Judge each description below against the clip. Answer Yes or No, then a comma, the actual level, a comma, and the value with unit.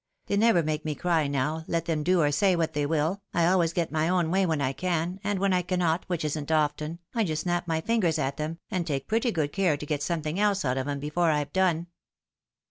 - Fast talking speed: Yes, fast, 245 wpm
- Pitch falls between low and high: Yes, medium, 165 Hz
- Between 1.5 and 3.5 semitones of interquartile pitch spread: Yes, average, 3.2 semitones